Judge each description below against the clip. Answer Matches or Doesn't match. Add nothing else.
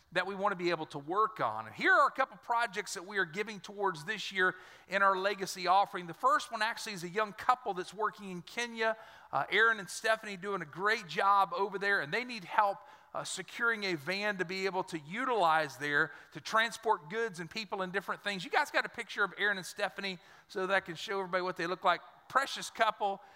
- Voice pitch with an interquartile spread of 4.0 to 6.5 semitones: Doesn't match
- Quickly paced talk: Matches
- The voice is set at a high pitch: Matches